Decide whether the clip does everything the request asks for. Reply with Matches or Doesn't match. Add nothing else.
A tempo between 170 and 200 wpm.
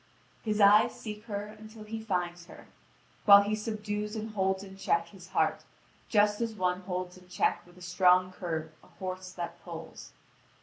Matches